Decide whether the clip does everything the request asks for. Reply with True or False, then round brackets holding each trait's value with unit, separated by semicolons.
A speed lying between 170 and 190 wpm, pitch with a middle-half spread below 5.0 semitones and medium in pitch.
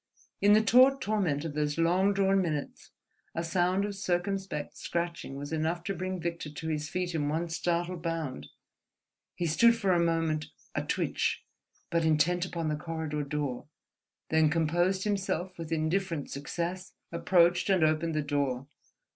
False (155 wpm; 3.1 semitones; 170 Hz)